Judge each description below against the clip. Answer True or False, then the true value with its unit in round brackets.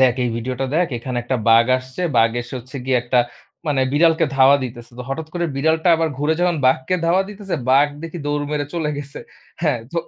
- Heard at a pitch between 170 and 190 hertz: False (140 Hz)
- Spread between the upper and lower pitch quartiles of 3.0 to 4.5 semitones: True (4.1 semitones)